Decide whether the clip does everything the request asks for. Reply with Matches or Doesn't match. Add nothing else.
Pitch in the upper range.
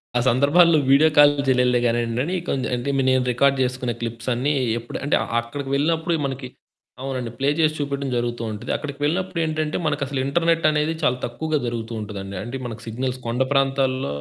Doesn't match